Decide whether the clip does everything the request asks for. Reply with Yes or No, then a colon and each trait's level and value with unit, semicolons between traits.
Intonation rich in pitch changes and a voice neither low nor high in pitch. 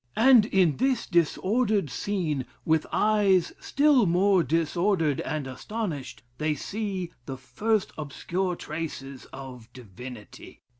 Yes: wide, 6.7 semitones; medium, 170 Hz